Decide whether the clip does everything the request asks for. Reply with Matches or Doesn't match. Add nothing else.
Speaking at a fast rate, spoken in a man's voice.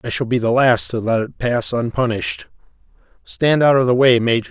Matches